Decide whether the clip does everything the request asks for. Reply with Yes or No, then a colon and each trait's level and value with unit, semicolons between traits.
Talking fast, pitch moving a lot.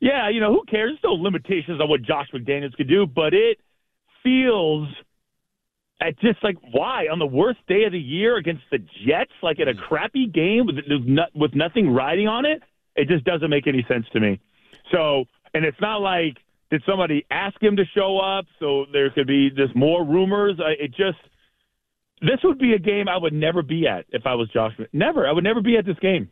Yes: fast, 215 wpm; wide, 6.0 semitones